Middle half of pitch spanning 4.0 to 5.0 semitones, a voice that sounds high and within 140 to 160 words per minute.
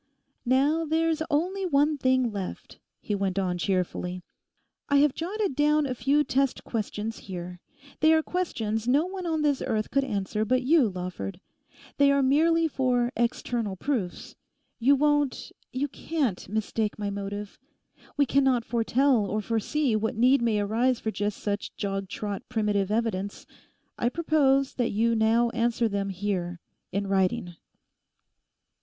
No: wide, 5.6 semitones; high, 235 Hz; average, 150 wpm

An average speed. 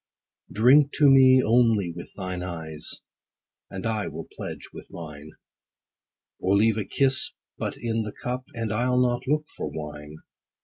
Yes: average, 150 wpm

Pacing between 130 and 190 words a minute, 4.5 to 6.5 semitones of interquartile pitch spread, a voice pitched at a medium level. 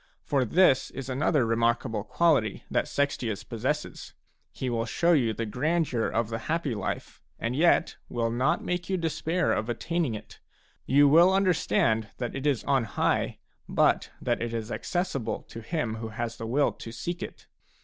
No: average, 170 wpm; wide, 5.6 semitones; low, 130 Hz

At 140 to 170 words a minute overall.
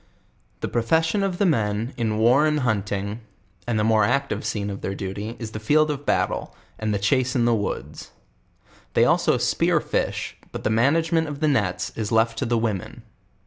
No: average, 195 wpm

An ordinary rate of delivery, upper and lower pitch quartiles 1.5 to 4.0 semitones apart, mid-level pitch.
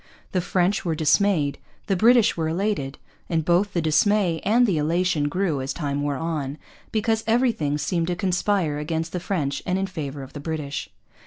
No: average, 180 wpm; average, 4.8 semitones; medium, 170 Hz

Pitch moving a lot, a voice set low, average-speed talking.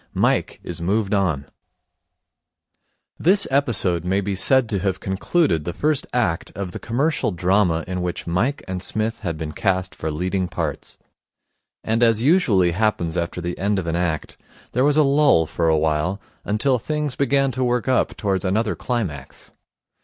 Yes: wide, 5.9 semitones; low, 100 Hz; average, 170 wpm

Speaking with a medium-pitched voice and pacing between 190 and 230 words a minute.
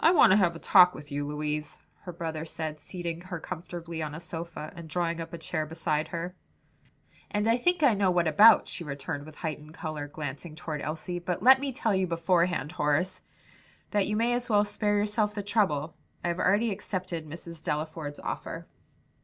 Yes: medium, 170 Hz; average, 195 wpm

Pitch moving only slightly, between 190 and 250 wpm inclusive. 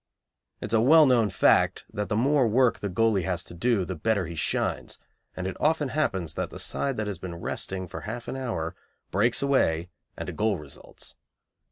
No: wide, 5.6 semitones; fast, 205 wpm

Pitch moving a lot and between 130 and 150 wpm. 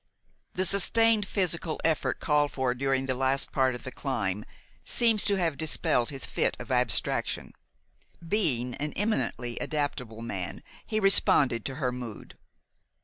Yes: wide, 6.4 semitones; average, 145 wpm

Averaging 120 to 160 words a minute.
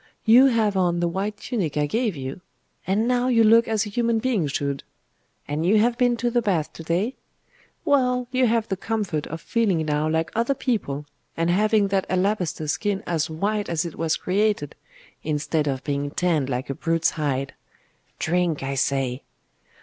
No: average, 180 wpm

